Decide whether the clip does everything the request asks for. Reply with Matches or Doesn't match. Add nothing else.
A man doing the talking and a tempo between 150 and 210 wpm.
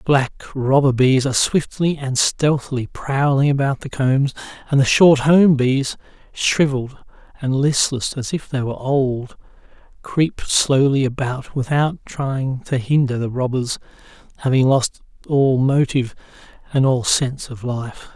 Doesn't match